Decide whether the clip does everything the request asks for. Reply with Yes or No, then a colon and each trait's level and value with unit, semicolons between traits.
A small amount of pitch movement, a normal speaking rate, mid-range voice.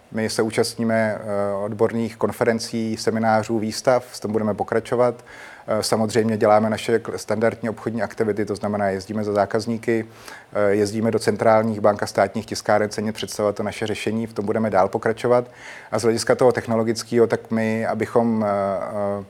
No: narrow, 1.5 semitones; average, 145 wpm; low, 110 Hz